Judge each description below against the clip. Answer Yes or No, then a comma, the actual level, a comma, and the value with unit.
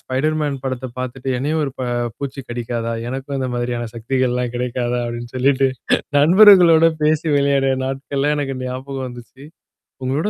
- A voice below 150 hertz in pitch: Yes, low, 135 Hz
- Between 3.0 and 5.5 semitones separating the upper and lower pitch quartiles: No, narrow, 2.4 semitones